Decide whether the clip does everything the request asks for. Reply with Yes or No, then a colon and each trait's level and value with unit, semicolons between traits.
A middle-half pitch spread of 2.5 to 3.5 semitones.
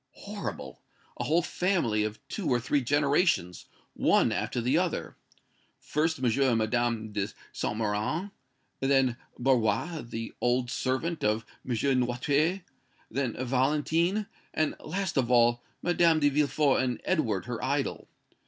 No: average, 4.8 semitones